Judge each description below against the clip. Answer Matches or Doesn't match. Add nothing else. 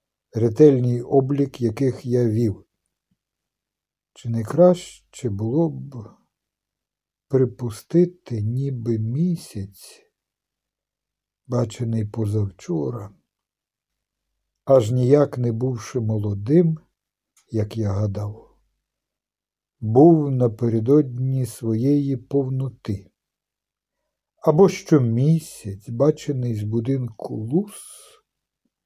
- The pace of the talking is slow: Matches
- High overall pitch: Doesn't match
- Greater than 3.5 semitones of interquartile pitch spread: Matches